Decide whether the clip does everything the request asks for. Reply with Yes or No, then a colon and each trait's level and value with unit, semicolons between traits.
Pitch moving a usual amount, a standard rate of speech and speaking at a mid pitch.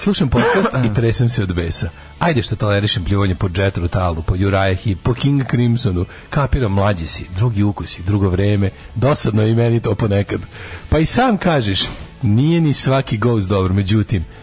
No: average, 3.7 semitones; average, 175 wpm; low, 105 Hz